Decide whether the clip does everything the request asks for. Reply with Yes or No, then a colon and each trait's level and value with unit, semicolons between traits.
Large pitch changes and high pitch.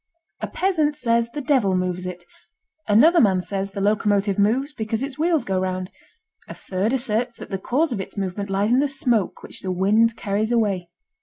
No: average, 5.0 semitones; high, 215 Hz